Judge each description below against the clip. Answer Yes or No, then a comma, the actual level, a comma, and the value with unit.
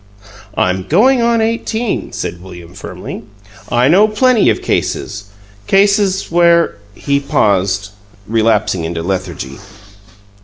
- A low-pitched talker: Yes, low, 120 Hz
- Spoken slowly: Yes, slow, 115 wpm